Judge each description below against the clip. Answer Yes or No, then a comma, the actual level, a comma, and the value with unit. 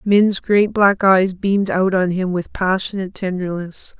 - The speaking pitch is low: No, high, 190 Hz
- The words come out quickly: No, average, 165 wpm